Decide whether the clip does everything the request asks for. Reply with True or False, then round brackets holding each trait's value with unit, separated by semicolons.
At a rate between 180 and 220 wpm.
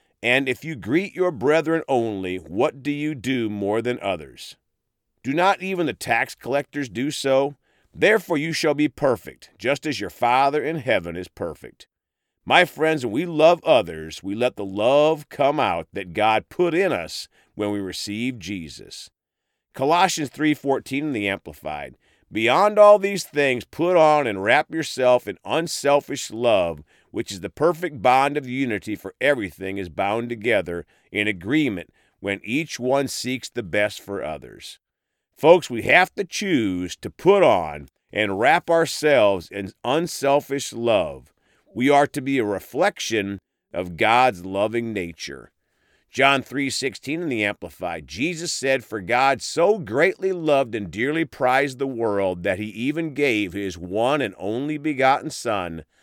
False (155 wpm)